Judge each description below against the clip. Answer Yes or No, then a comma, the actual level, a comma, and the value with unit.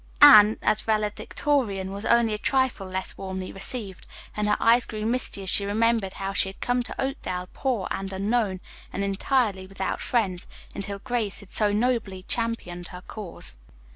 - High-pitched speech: Yes, high, 210 Hz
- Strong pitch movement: No, average, 3.4 semitones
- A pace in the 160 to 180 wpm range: Yes, average, 170 wpm